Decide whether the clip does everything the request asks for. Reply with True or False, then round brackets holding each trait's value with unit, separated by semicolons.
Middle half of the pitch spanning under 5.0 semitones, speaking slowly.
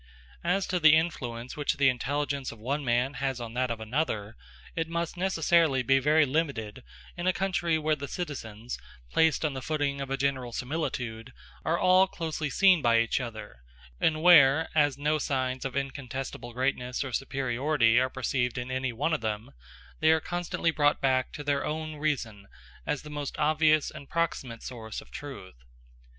False (4.0 semitones; 175 wpm)